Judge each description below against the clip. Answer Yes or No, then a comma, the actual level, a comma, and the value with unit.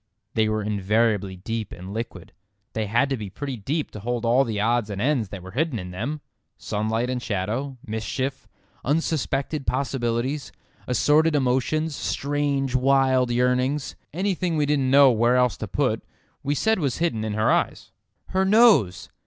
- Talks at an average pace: Yes, average, 160 wpm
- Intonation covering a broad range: No, average, 4.6 semitones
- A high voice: No, low, 125 Hz